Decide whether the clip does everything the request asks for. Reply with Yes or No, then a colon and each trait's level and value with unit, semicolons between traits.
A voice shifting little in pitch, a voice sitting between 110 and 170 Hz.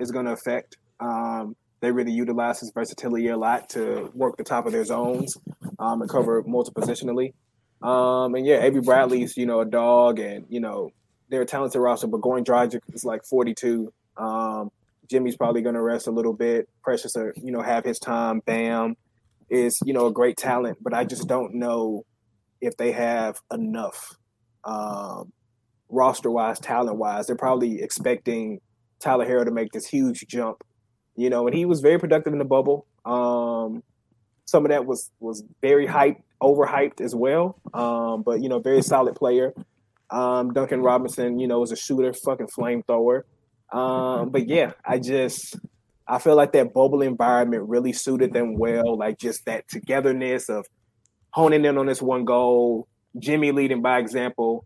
Yes: narrow, 1.9 semitones; low, 120 Hz